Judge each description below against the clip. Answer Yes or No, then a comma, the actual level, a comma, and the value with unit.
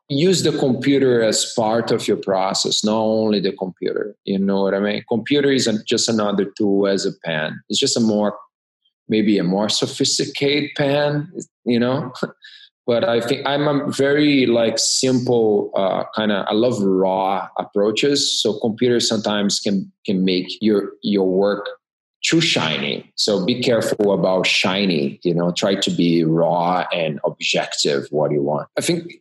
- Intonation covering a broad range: Yes, wide, 6.0 semitones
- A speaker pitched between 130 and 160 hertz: No, low, 110 Hz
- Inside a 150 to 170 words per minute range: Yes, average, 165 wpm